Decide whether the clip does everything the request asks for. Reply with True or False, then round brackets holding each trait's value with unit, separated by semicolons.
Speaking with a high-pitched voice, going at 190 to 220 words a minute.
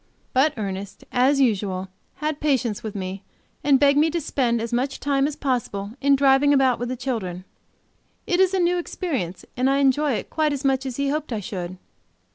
True (265 Hz; 200 wpm)